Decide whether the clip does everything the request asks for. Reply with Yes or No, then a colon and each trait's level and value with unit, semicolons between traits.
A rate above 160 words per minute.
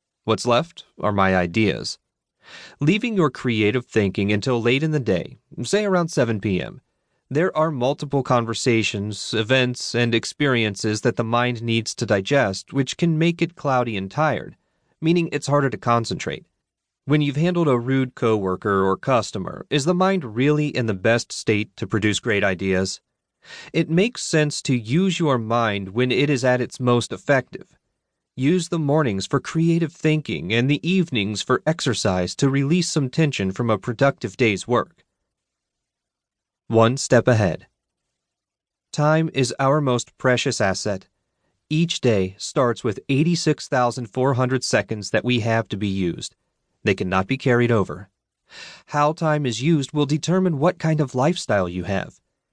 No: average, 155 wpm